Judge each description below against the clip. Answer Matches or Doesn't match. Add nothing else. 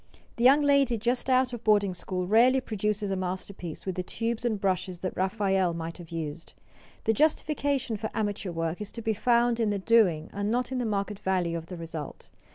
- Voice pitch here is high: Matches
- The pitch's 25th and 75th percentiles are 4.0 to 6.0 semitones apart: Matches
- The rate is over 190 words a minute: Matches